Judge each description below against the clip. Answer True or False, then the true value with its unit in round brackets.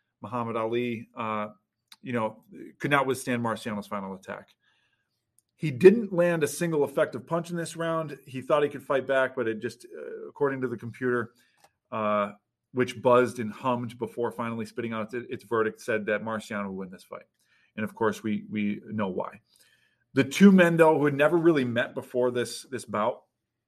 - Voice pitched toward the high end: False (125 Hz)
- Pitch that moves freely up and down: False (4.6 semitones)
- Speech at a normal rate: True (190 wpm)